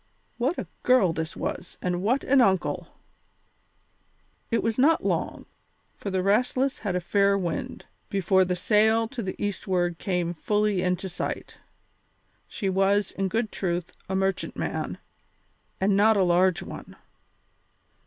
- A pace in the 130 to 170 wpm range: Yes, average, 140 wpm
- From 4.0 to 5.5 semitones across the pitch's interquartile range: No, average, 3.2 semitones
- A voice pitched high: Yes, high, 195 Hz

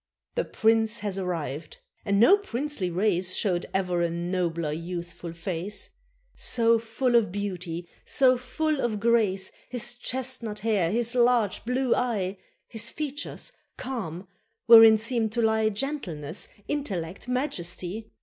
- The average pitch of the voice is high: Yes, high, 215 Hz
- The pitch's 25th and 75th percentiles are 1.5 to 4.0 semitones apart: No, average, 5.1 semitones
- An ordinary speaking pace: No, slow, 130 wpm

